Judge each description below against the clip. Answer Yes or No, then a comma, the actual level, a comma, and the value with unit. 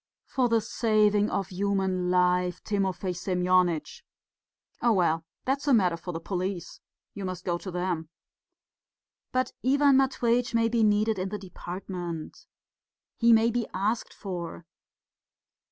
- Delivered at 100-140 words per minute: Yes, slow, 135 wpm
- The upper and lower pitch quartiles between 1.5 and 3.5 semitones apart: No, average, 4.1 semitones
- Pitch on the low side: No, high, 190 Hz